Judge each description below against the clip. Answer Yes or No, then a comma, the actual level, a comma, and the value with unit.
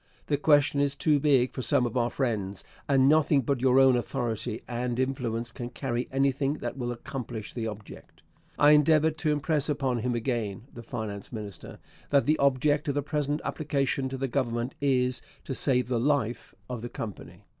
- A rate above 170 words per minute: Yes, average, 185 wpm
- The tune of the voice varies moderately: Yes, average, 3.2 semitones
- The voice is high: No, low, 130 Hz